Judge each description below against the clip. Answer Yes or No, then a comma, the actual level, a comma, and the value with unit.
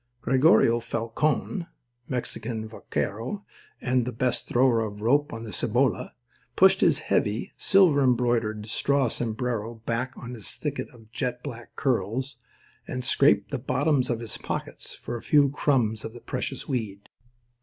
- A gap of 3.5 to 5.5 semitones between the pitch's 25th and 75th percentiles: No, average, 2.9 semitones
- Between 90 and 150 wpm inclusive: Yes, average, 145 wpm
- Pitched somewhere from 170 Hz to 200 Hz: No, low, 120 Hz